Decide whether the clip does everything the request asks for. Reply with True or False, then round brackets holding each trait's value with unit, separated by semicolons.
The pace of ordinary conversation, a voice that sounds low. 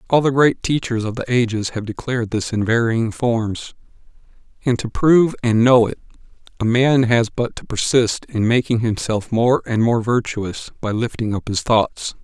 True (180 wpm; 115 Hz)